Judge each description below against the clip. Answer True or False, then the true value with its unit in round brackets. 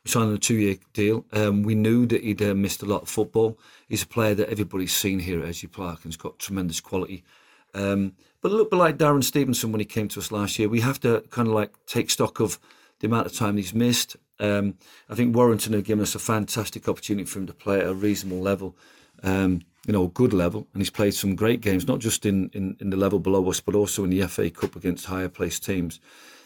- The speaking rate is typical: False (245 wpm)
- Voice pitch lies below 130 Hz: True (105 Hz)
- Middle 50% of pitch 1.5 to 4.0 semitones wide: True (2.7 semitones)